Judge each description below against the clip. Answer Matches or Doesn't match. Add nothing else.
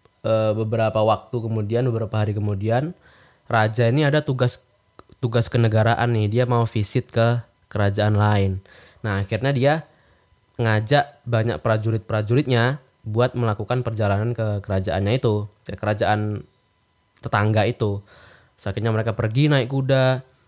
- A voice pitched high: Doesn't match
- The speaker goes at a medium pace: Matches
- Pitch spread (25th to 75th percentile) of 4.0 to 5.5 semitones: Doesn't match